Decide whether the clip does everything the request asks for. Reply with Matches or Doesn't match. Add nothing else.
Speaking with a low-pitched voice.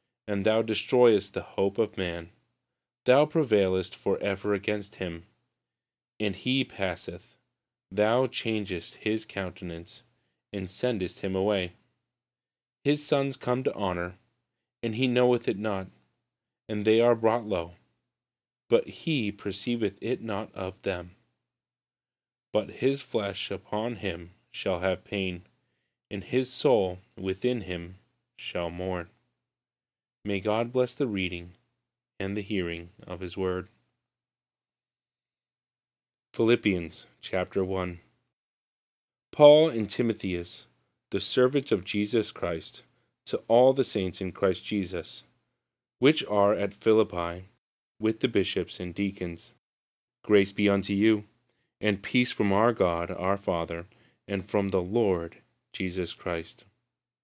Matches